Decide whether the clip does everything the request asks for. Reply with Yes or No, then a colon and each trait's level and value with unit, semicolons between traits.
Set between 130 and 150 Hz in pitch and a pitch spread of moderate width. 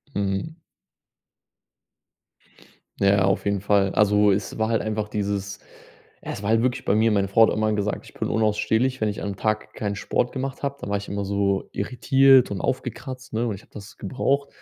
No: low, 105 Hz; average, 3.2 semitones